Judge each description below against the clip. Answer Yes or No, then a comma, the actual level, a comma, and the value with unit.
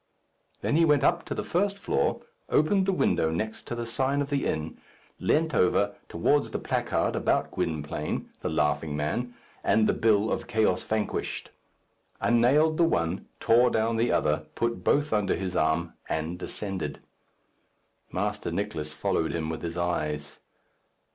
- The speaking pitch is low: Yes, low, 105 Hz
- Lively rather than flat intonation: Yes, wide, 8.4 semitones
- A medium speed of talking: Yes, average, 155 wpm